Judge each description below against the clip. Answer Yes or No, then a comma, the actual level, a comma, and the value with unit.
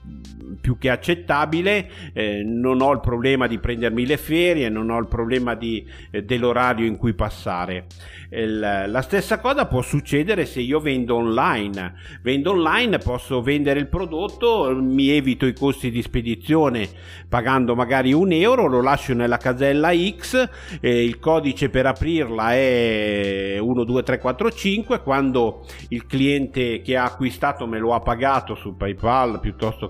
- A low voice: Yes, low, 125 Hz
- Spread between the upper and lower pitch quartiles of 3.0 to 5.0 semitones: Yes, average, 3.5 semitones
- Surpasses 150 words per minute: No, average, 145 wpm